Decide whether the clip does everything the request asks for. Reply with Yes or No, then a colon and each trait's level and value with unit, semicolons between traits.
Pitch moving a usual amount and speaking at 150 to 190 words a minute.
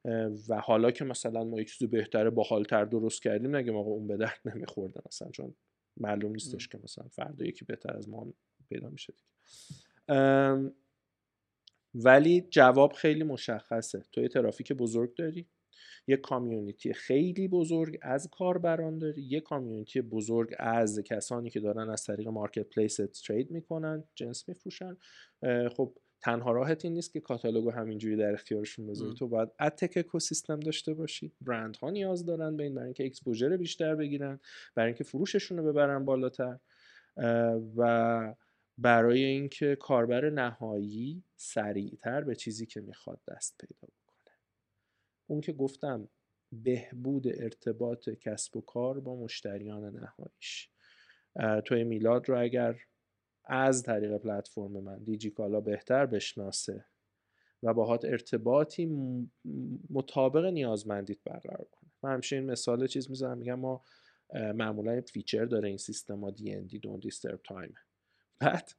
No: average, 4.2 semitones; average, 140 wpm